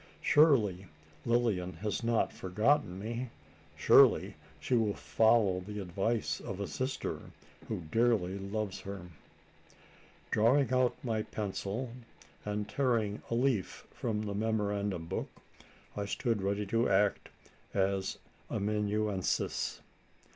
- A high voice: No, low, 105 Hz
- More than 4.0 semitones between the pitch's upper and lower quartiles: No, average, 3.0 semitones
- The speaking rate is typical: No, slow, 110 wpm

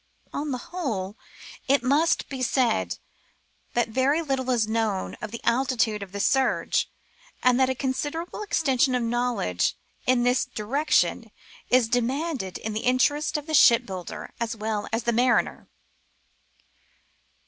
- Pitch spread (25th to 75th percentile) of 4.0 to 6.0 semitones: No, average, 3.5 semitones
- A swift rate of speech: No, average, 145 wpm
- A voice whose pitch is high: Yes, high, 245 Hz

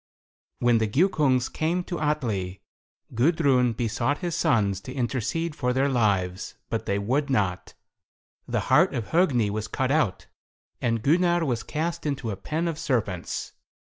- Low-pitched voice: Yes, low, 125 Hz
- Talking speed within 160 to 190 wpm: No, average, 150 wpm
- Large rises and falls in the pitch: Yes, wide, 6.0 semitones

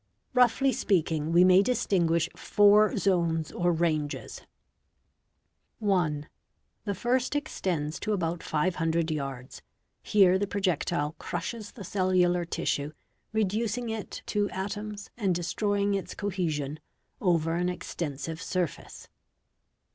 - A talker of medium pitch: Yes, medium, 180 Hz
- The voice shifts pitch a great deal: No, average, 3.9 semitones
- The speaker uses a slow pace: Yes, slow, 115 wpm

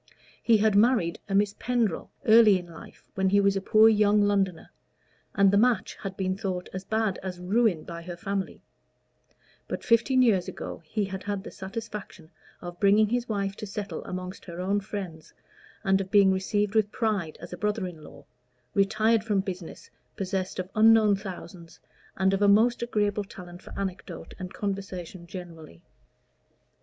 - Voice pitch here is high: Yes, high, 195 Hz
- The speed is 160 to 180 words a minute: Yes, average, 170 wpm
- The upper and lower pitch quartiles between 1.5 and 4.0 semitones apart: Yes, narrow, 2.4 semitones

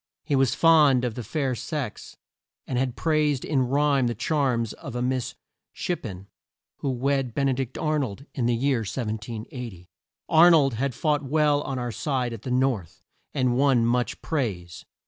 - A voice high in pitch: No, low, 130 Hz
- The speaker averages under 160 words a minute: No, average, 180 wpm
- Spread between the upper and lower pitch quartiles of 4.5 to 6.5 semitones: No, average, 3.2 semitones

